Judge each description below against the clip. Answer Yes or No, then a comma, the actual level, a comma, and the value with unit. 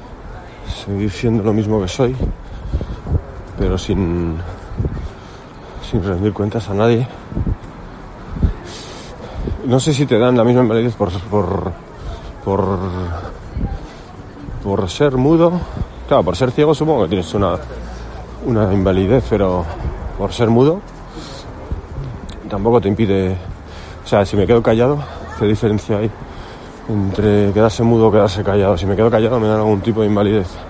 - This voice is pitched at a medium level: No, low, 105 Hz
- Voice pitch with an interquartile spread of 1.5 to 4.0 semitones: Yes, average, 3.4 semitones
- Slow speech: No, average, 135 wpm